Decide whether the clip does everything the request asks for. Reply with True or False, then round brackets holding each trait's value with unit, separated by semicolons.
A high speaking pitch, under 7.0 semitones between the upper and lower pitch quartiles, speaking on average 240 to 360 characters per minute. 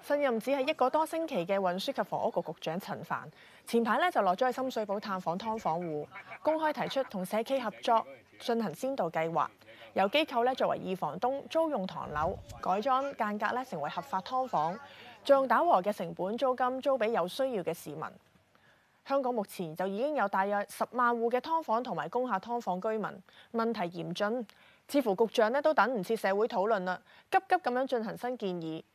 True (230 Hz; 5.6 semitones; 295 characters per minute)